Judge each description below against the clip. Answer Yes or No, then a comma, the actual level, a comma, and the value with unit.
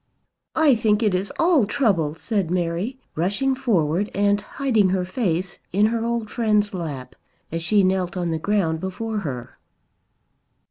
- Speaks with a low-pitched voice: No, high, 200 Hz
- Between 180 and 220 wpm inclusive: No, average, 150 wpm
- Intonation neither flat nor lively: Yes, average, 4.4 semitones